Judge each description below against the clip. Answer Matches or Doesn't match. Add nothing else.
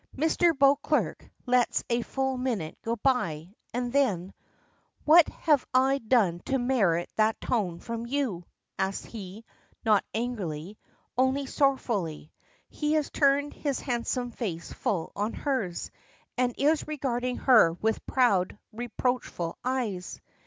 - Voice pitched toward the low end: Doesn't match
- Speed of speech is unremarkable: Doesn't match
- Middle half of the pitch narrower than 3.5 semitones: Doesn't match